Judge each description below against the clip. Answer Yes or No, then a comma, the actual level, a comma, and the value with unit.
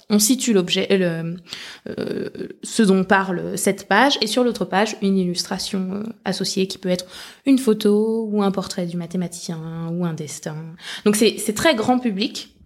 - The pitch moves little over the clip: No, average, 3.2 semitones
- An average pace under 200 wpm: Yes, average, 180 wpm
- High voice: Yes, high, 195 Hz